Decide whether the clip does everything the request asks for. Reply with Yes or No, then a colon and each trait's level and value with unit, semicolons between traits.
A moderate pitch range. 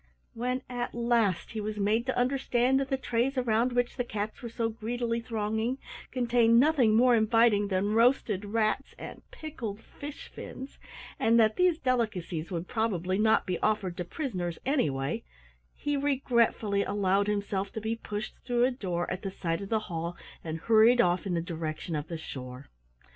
Yes: average, 4.1 semitones